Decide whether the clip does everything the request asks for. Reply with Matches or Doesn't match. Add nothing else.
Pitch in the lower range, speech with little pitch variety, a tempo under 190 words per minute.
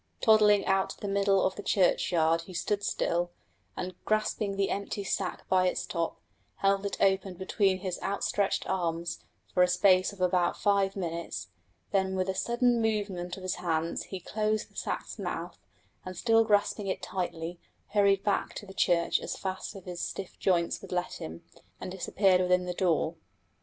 Doesn't match